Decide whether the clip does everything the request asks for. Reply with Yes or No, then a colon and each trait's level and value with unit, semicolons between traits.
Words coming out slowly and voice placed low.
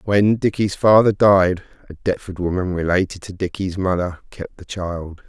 No: average, 160 wpm; very low, 95 Hz